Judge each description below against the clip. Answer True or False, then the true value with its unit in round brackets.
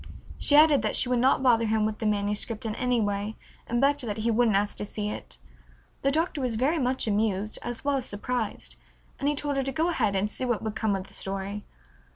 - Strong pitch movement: False (4.1 semitones)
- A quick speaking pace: True (235 wpm)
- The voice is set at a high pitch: True (225 Hz)